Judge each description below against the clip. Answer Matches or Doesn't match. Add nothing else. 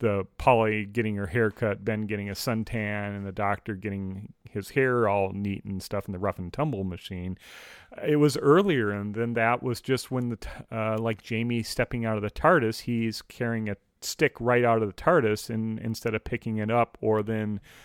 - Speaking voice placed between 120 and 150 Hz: Doesn't match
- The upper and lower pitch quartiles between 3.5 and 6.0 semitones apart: Doesn't match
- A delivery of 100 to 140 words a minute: Doesn't match